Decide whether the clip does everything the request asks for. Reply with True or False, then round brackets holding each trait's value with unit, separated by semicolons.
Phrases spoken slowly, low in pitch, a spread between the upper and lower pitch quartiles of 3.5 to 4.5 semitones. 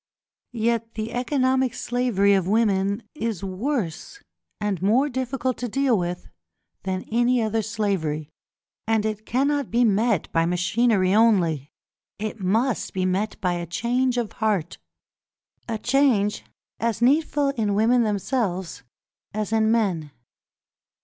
False (130 wpm; 220 Hz; 4.1 semitones)